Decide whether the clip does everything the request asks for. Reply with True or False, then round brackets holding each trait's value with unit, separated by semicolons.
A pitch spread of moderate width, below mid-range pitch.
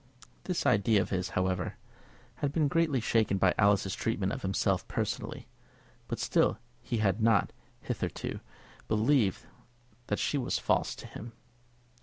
True (4.4 semitones; 110 Hz)